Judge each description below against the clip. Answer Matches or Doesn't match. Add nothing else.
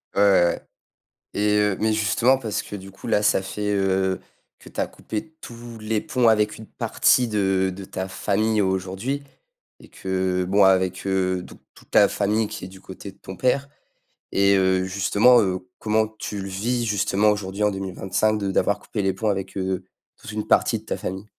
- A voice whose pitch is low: Matches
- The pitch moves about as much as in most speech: Doesn't match